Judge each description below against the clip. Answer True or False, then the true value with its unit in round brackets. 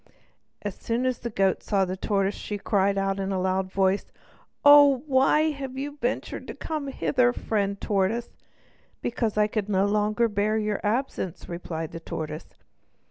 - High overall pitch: True (210 Hz)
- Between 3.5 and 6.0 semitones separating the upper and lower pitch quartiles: True (4.1 semitones)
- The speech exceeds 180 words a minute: False (165 wpm)